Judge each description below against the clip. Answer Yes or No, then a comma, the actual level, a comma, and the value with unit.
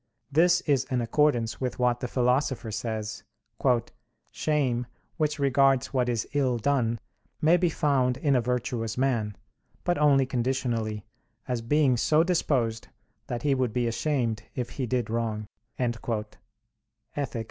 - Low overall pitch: Yes, low, 125 Hz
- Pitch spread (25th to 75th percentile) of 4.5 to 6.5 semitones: No, average, 3.3 semitones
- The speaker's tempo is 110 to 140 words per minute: Yes, slow, 135 wpm